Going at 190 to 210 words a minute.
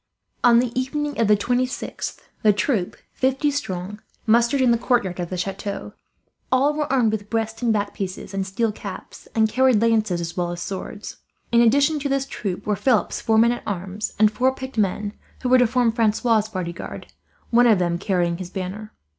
Yes: average, 195 wpm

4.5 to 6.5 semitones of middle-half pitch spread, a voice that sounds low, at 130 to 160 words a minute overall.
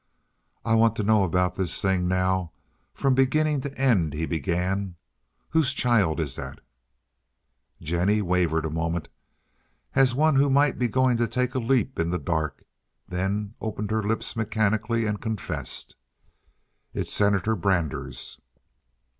Yes: average, 5.0 semitones; low, 105 Hz; average, 140 wpm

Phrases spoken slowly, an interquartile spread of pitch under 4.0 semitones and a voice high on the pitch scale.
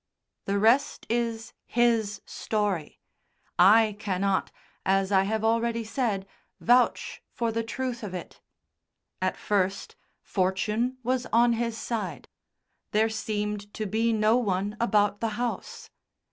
Yes: slow, 125 wpm; narrow, 2.5 semitones; high, 220 Hz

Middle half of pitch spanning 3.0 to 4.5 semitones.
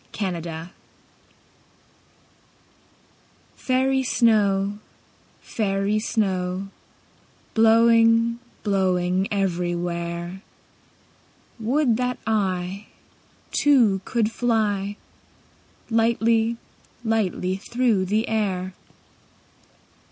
Yes: average, 3.4 semitones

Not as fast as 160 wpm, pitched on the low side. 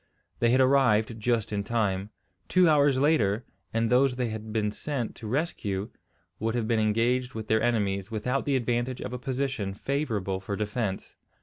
No: average, 175 wpm; low, 115 Hz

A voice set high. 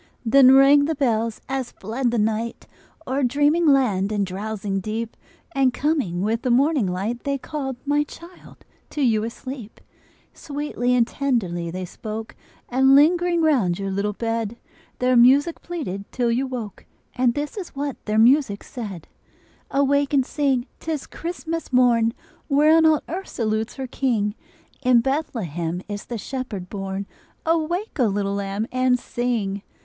Yes: high, 245 Hz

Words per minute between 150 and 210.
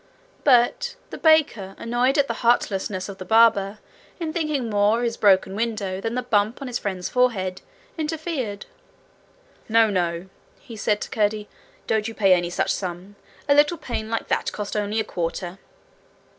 Yes: average, 170 wpm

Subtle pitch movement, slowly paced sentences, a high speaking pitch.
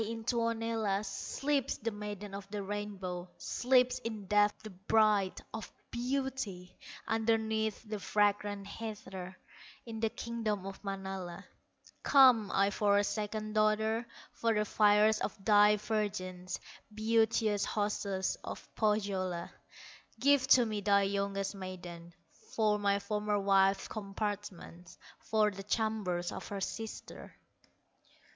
Yes: narrow, 2.0 semitones; slow, 120 wpm; high, 210 Hz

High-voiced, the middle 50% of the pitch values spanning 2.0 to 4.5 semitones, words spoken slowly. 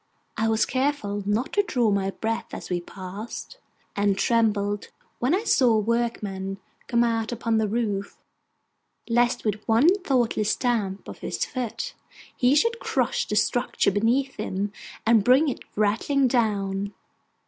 No: high, 225 Hz; average, 3.4 semitones; average, 150 wpm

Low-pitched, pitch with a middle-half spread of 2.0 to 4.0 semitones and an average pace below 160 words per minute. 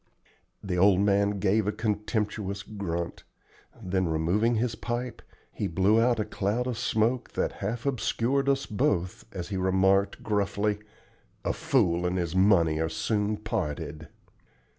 Yes: low, 100 Hz; average, 3.3 semitones; average, 140 wpm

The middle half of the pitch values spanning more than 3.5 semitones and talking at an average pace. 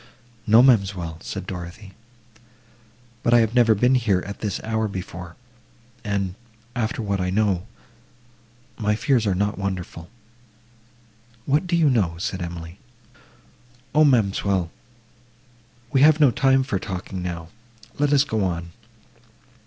No: average, 4.6 semitones; slow, 125 wpm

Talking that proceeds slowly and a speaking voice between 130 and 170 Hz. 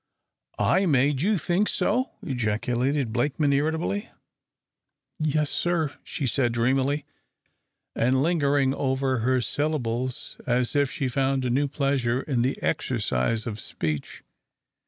Yes: slow, 120 wpm; low, 135 Hz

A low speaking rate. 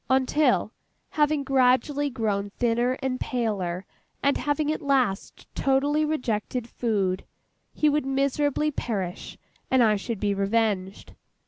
Yes: slow, 120 wpm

